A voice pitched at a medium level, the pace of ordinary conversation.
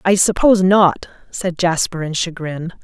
Yes: medium, 175 Hz; average, 150 wpm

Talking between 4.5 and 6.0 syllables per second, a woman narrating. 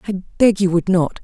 Yes: 4.7 syllables/s; female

